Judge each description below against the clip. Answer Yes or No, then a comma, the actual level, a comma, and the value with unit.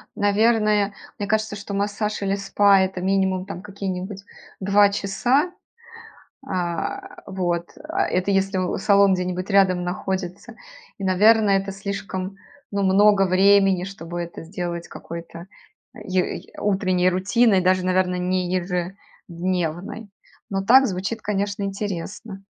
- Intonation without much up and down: Yes, narrow, 1.8 semitones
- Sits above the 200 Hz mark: No, high, 195 Hz